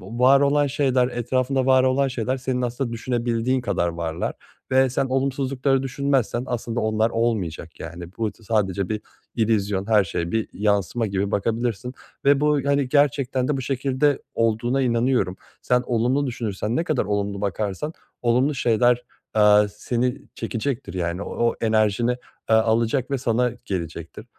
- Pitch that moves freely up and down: No, average, 3.8 semitones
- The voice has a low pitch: Yes, low, 120 Hz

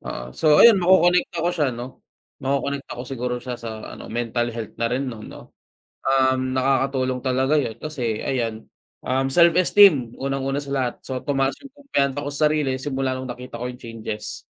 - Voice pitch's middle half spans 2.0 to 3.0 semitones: Yes, narrow, 2.6 semitones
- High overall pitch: No, low, 130 Hz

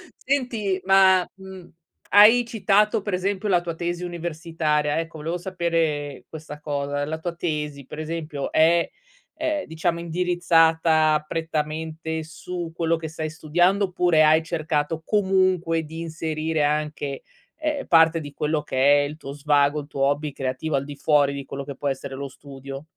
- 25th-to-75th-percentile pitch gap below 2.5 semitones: No, average, 2.9 semitones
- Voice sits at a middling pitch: Yes, medium, 160 Hz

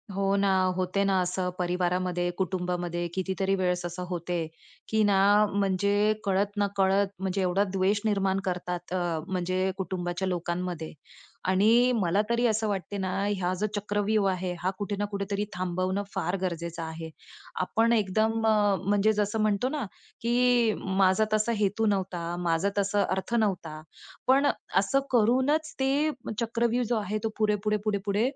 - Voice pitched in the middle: No, high, 195 Hz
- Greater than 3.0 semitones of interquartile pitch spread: No, average, 2.7 semitones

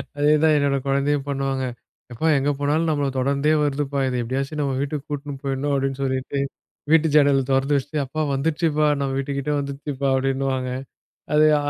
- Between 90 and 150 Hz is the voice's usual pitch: Yes, medium, 140 Hz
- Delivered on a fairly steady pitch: Yes, narrow, 1.4 semitones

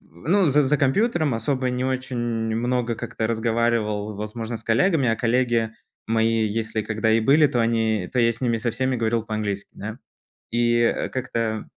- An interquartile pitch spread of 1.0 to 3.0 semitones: Yes, narrow, 2.4 semitones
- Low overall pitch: Yes, low, 115 Hz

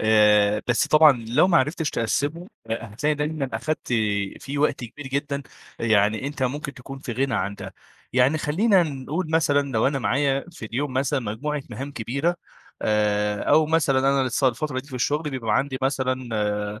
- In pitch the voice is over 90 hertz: Yes, low, 135 Hz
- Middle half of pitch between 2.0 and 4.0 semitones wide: No, average, 4.5 semitones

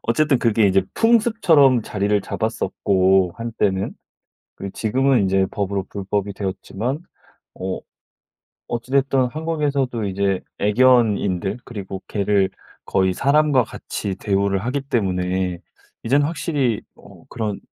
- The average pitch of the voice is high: No, low, 105 Hz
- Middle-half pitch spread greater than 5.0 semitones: Yes, wide, 5.6 semitones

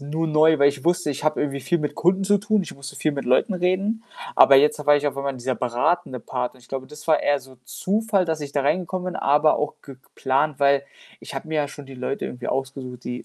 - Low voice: No, medium, 145 Hz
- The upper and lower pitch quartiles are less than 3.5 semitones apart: No, average, 3.8 semitones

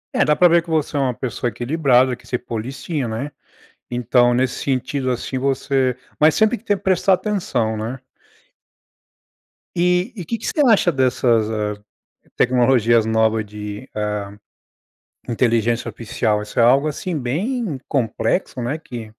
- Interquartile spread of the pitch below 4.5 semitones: No, average, 5.0 semitones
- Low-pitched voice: Yes, low, 130 Hz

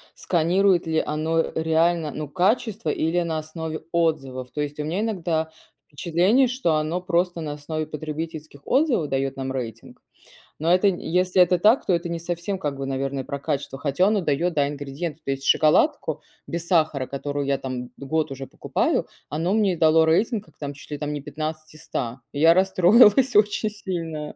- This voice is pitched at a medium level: Yes, medium, 160 Hz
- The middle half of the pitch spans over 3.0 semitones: Yes, average, 3.7 semitones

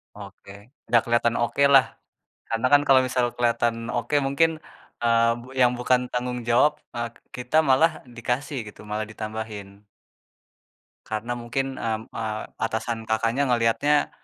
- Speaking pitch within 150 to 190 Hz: No, low, 120 Hz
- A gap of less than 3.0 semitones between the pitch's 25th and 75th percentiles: Yes, narrow, 2.5 semitones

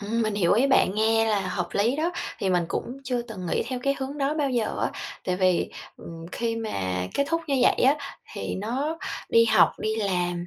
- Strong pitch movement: Yes, wide, 6.2 semitones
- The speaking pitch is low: No, high, 225 Hz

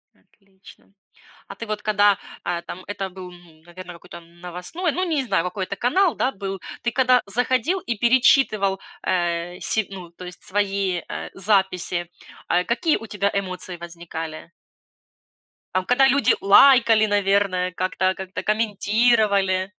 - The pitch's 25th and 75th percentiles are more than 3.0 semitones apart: Yes, average, 3.8 semitones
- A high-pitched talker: Yes, high, 195 Hz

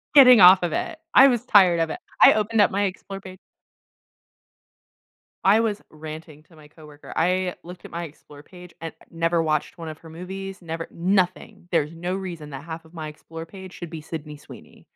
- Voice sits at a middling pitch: Yes, medium, 170 Hz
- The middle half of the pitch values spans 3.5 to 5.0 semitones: No, average, 3.1 semitones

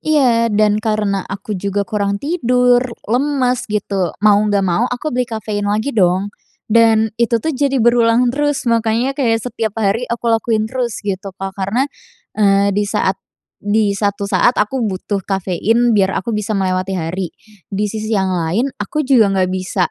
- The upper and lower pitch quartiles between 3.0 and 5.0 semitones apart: Yes, average, 3.4 semitones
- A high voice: Yes, high, 215 Hz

